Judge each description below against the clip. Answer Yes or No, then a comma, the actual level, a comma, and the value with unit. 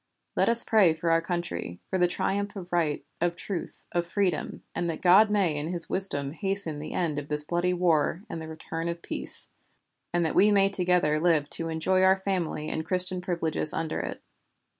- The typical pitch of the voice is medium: Yes, medium, 175 Hz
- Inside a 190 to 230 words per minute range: Yes, average, 200 wpm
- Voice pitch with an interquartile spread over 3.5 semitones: No, average, 2.8 semitones